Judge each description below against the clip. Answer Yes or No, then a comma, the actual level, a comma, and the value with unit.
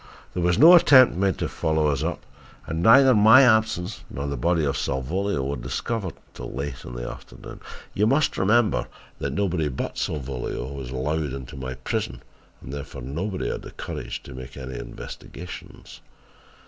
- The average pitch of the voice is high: No, very low, 80 Hz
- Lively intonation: Yes, wide, 7.3 semitones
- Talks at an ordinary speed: Yes, average, 170 wpm